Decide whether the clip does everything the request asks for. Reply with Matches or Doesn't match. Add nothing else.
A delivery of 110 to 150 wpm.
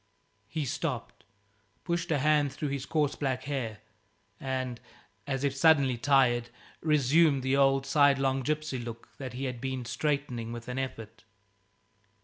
Matches